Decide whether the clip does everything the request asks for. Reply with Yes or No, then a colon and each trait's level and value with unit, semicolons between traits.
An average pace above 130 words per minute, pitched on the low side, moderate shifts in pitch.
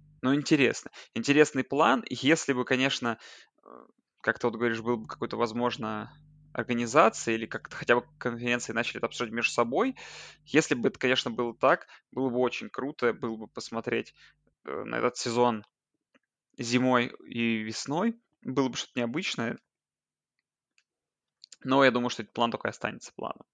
No: average, 145 wpm; low, 120 Hz; narrow, 2.3 semitones